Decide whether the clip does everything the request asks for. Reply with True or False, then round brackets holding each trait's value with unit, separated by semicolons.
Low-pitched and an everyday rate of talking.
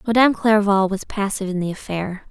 False (200 Hz; 180 wpm)